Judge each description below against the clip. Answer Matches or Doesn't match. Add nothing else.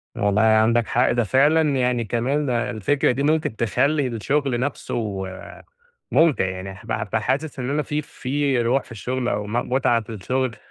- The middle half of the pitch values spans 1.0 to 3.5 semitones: Doesn't match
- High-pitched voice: Doesn't match